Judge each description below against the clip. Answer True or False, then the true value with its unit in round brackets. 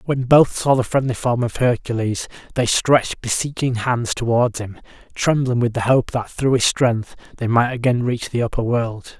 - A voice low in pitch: True (120 Hz)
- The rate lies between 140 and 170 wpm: False (190 wpm)